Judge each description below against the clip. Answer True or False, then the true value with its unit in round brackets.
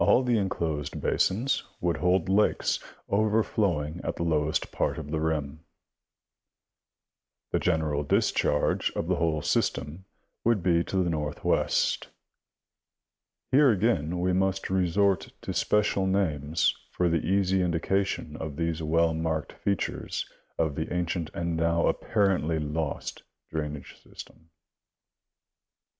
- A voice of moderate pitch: False (85 Hz)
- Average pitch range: True (3.5 semitones)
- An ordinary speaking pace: False (120 wpm)